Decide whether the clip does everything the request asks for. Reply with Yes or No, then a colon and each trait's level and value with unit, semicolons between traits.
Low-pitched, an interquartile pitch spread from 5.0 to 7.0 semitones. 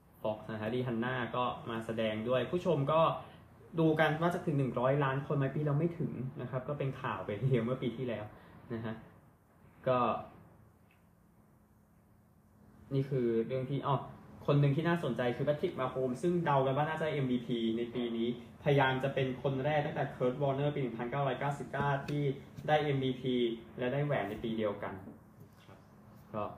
No: low, 130 Hz; average, 3.3 semitones